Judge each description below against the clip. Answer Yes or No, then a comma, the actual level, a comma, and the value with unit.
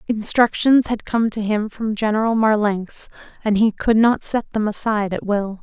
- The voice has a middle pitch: No, high, 215 Hz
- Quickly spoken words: No, average, 180 wpm